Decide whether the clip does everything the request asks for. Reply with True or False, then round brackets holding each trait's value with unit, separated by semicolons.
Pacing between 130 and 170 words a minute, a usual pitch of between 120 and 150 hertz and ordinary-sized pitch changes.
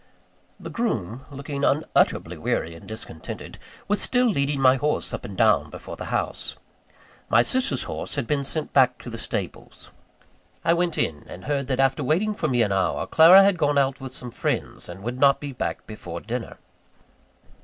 False (185 wpm; 135 Hz; 4.4 semitones)